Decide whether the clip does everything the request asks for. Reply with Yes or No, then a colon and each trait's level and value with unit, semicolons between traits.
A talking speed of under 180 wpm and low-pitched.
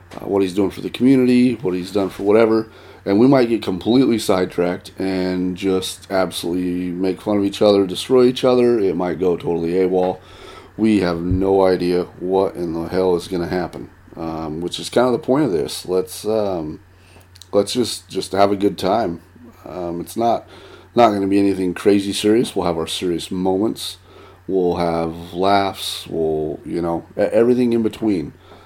No: average, 185 wpm; very low, 95 Hz